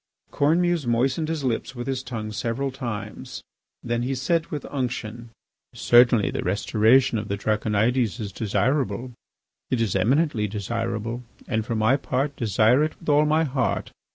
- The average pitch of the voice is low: Yes, low, 120 Hz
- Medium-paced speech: Yes, average, 155 wpm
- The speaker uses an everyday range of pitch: Yes, average, 3.9 semitones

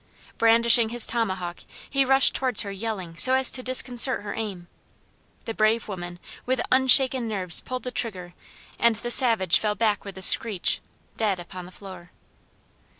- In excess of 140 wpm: Yes, average, 160 wpm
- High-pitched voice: Yes, high, 220 Hz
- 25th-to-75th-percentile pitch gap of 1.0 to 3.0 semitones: No, average, 4.7 semitones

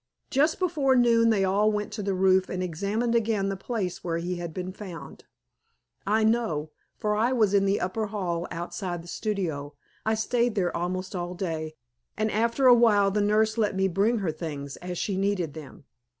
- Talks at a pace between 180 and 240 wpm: Yes, average, 195 wpm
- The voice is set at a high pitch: Yes, high, 195 Hz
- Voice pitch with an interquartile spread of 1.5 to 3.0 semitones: No, average, 3.7 semitones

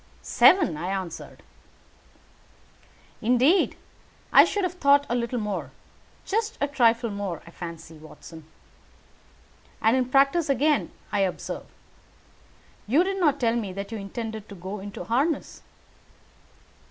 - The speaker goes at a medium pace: No, slow, 130 wpm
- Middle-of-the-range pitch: No, high, 230 Hz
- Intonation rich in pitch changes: Yes, wide, 6.4 semitones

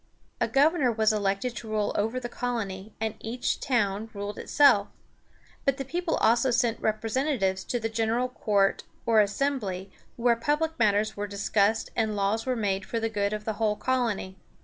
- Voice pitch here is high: Yes, high, 220 Hz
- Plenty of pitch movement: No, average, 3.3 semitones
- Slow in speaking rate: No, average, 170 wpm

